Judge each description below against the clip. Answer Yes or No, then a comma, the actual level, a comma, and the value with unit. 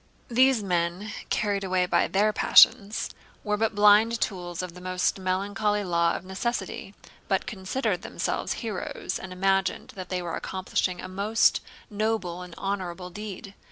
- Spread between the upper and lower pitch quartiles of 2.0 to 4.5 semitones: Yes, narrow, 2.4 semitones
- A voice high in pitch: Yes, high, 195 Hz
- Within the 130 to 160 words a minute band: Yes, average, 150 wpm